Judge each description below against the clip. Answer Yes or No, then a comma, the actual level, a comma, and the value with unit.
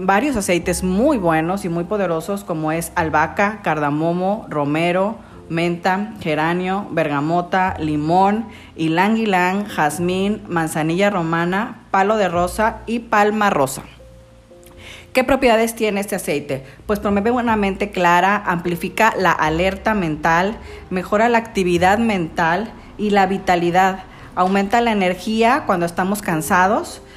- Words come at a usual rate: No, slow, 120 wpm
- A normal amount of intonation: Yes, average, 3.6 semitones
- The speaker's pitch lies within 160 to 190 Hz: Yes, medium, 185 Hz